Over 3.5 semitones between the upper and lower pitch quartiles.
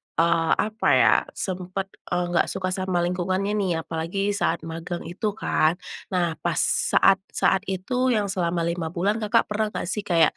No: average, 2.9 semitones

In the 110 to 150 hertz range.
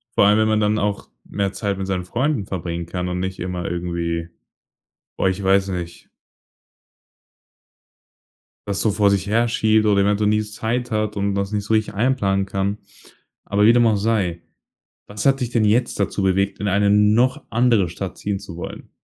No: low, 100 Hz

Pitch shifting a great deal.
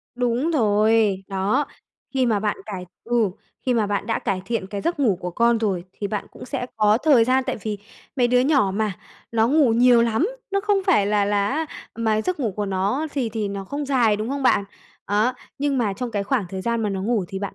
No: average, 3.9 semitones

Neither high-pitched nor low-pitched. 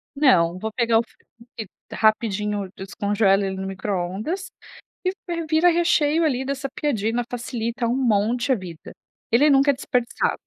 No: high, 235 Hz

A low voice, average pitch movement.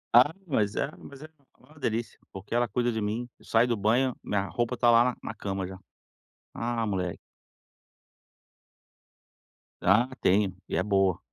Yes: low, 115 Hz; average, 3.6 semitones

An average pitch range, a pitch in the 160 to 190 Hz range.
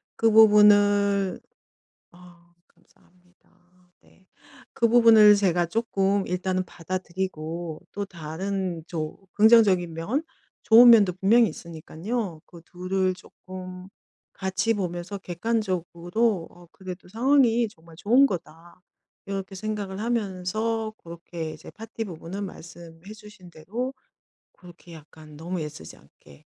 Yes: average, 3.4 semitones; medium, 185 Hz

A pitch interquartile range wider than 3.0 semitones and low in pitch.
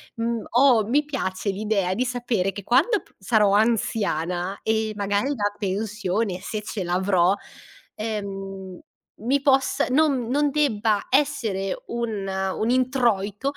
No: average, 4.1 semitones; high, 215 Hz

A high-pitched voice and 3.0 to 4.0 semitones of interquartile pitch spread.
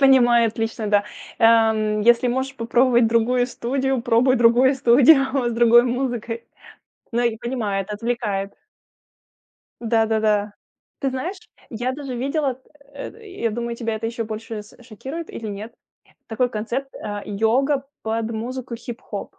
No: high, 235 Hz; narrow, 2.6 semitones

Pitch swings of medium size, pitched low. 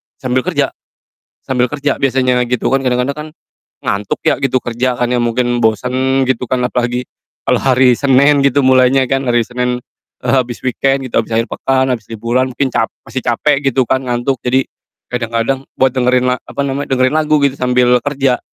No: narrow, 1.5 semitones; low, 125 Hz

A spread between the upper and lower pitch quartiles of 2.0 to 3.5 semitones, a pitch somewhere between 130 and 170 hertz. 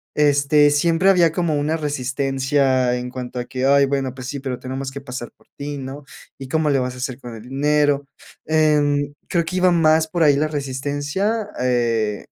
Yes: average, 2.7 semitones; medium, 140 Hz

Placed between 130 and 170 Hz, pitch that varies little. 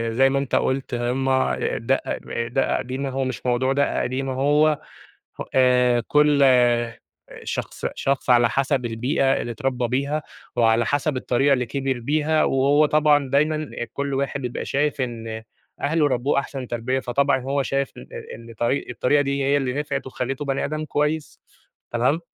Yes: low, 135 Hz; narrow, 2.3 semitones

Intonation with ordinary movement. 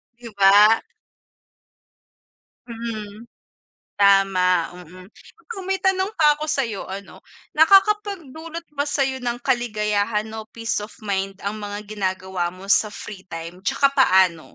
No: wide, 6.0 semitones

